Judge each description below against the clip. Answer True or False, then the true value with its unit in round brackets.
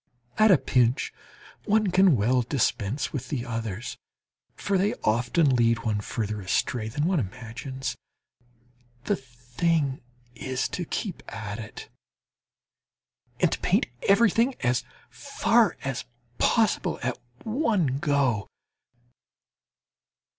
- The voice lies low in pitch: True (130 Hz)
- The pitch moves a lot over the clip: True (7.6 semitones)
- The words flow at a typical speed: False (110 wpm)